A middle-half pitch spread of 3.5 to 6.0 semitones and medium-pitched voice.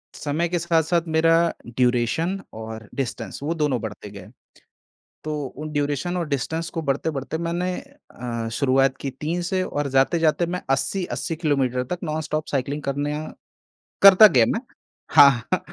Yes: average, 3.9 semitones; medium, 150 Hz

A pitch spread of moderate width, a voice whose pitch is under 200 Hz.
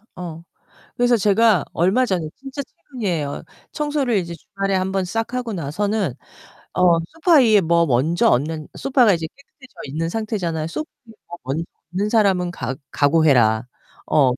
No: wide, 5.9 semitones; medium, 185 Hz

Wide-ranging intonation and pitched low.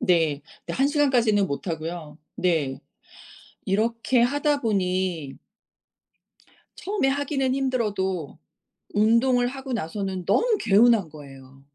No: wide, 7.7 semitones; high, 205 Hz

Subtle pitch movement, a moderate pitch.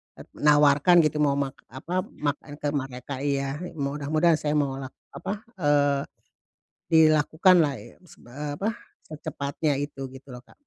Yes: narrow, 1.9 semitones; medium, 145 Hz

